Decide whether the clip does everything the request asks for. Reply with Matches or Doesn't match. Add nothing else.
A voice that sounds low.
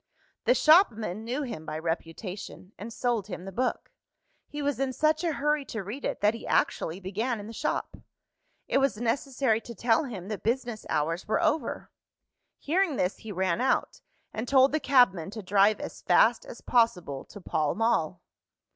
Doesn't match